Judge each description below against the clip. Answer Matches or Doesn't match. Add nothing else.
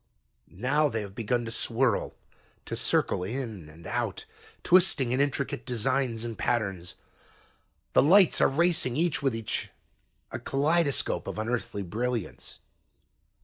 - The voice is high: Doesn't match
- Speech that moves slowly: Matches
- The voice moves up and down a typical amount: Matches